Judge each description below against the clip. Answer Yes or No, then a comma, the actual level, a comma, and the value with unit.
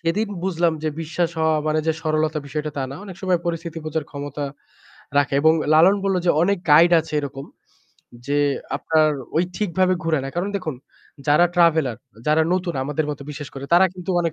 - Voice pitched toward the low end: No, medium, 160 Hz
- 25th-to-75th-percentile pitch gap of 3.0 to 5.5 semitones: No, narrow, 2.4 semitones